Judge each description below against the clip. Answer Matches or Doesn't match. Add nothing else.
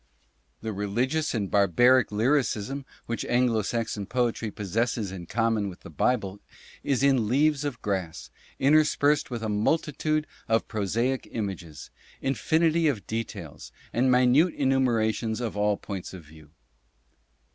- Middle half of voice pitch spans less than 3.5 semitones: Doesn't match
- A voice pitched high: Doesn't match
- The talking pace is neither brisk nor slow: Doesn't match